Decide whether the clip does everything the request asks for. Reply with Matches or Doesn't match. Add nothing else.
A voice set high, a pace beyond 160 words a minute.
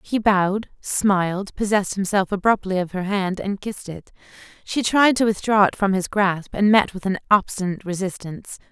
Matches